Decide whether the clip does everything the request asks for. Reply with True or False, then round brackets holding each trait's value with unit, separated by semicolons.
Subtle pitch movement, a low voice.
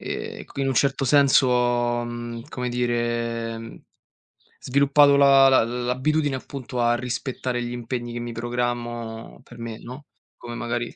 True (1.7 semitones; 120 Hz)